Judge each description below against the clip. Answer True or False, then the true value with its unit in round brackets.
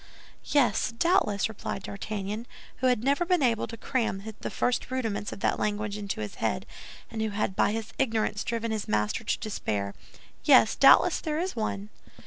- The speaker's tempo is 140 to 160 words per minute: False (175 wpm)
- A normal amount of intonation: True (3.5 semitones)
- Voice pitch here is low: False (220 Hz)